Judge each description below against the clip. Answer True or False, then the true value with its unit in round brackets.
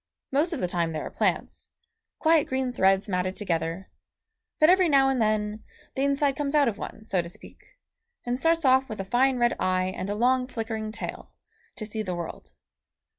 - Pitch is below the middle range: False (225 Hz)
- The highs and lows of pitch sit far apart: True (5.9 semitones)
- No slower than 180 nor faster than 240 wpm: True (195 wpm)